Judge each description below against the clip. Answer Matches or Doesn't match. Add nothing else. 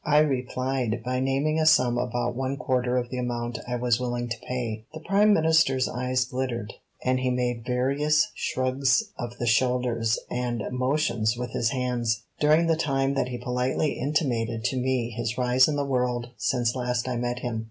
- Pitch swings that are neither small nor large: Doesn't match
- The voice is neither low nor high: Doesn't match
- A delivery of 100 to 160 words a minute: Doesn't match